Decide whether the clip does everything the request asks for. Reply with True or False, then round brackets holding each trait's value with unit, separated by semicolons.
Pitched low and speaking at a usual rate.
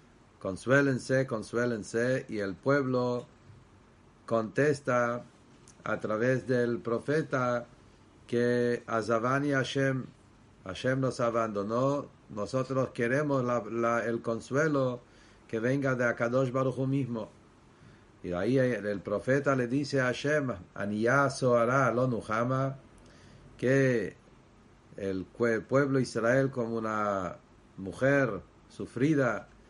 False (120 Hz; 105 wpm)